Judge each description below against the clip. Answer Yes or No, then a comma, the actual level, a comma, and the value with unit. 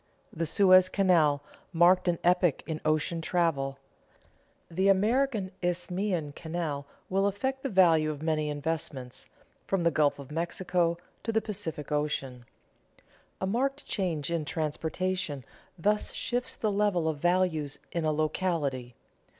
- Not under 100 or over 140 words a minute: Yes, slow, 135 wpm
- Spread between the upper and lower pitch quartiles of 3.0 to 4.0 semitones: Yes, average, 3.6 semitones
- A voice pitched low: No, medium, 170 Hz